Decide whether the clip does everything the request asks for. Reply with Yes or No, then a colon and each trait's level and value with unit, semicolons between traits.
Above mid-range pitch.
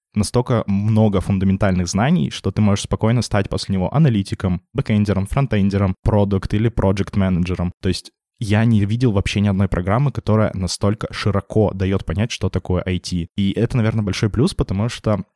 No: low, 100 Hz